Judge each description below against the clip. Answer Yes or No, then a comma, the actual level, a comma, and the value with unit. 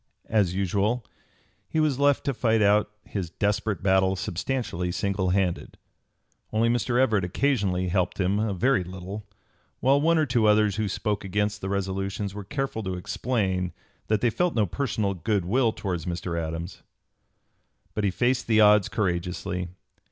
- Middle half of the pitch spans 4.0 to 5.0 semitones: No, average, 3.5 semitones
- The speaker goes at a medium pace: Yes, average, 160 wpm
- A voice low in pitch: Yes, low, 100 Hz